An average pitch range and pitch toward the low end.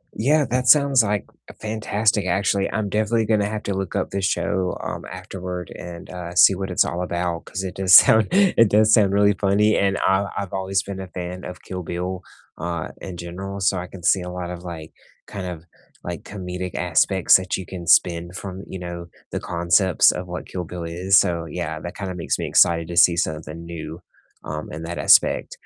No: narrow, 2.3 semitones; very low, 90 Hz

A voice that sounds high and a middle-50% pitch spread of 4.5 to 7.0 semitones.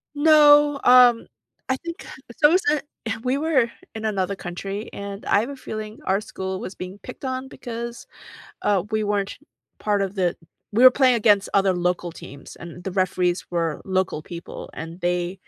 Yes: high, 205 Hz; wide, 5.4 semitones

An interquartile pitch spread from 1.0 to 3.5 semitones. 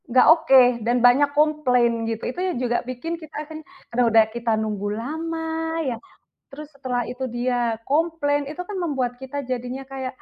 No: average, 3.9 semitones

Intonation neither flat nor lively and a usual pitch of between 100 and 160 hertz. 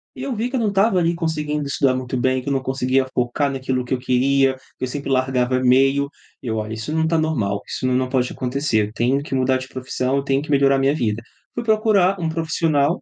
Yes: average, 3.6 semitones; low, 135 Hz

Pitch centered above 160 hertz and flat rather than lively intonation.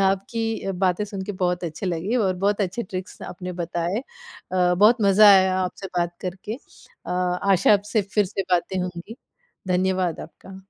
Yes: high, 190 Hz; narrow, 2.2 semitones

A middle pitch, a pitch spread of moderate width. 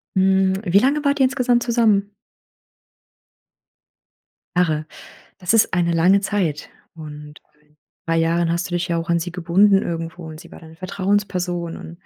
Yes: medium, 180 Hz; average, 3.3 semitones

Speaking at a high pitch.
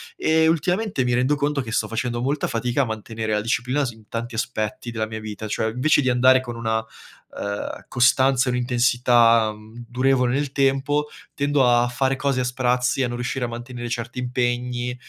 No: low, 125 Hz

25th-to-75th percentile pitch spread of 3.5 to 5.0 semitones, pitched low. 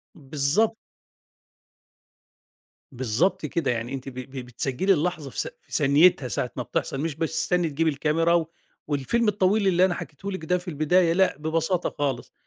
No: average, 4.6 semitones; medium, 160 Hz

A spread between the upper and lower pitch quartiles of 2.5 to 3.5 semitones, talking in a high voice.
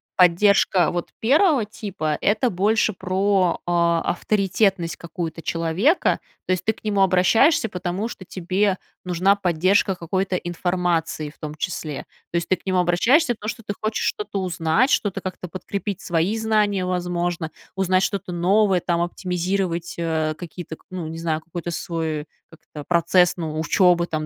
No: average, 2.9 semitones; medium, 180 Hz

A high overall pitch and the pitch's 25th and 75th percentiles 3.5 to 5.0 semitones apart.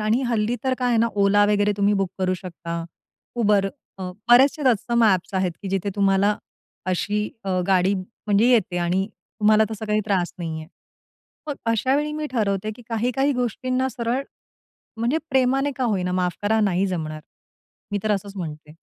Yes: high, 210 Hz; average, 4.2 semitones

